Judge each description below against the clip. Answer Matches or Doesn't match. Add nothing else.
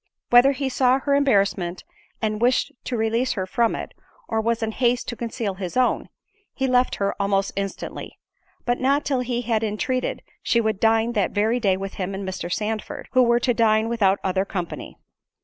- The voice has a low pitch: Doesn't match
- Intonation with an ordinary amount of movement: Matches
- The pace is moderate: Matches